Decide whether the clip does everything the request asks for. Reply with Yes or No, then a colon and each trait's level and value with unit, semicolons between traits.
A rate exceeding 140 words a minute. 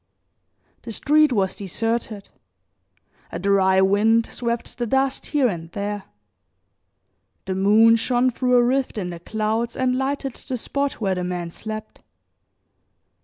No: slow, 135 wpm